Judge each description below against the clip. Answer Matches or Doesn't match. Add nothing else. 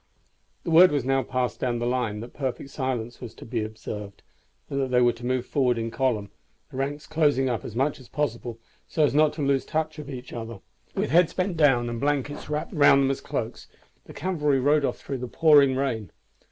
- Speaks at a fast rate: Matches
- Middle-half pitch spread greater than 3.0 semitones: Matches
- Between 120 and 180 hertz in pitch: Matches